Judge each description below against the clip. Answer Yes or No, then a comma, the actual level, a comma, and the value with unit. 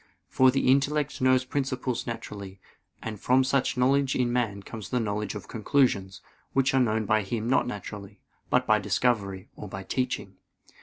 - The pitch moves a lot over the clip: No, average, 4.0 semitones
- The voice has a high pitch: No, low, 120 Hz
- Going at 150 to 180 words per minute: Yes, average, 165 wpm